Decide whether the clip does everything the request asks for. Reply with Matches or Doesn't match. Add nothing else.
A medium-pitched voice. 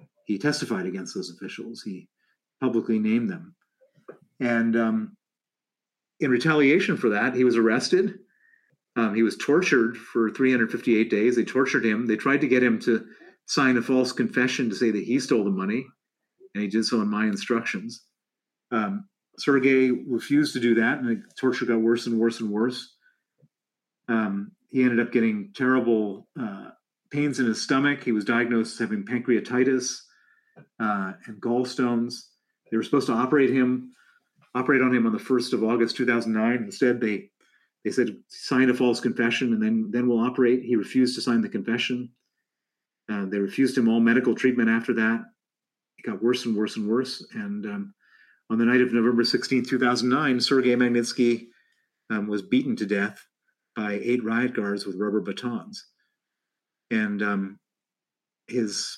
Doesn't match